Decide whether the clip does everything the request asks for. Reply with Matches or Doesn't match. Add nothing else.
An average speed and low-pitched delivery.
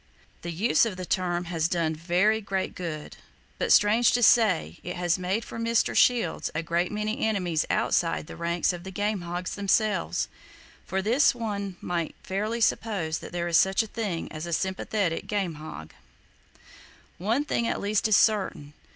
Doesn't match